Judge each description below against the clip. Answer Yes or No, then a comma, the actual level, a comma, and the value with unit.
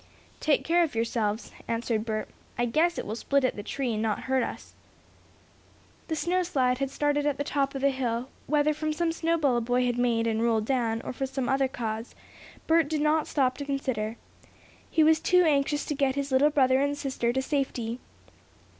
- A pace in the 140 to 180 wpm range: No, fast, 205 wpm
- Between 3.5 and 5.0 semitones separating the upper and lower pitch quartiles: Yes, average, 3.9 semitones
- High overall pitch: Yes, very high, 270 Hz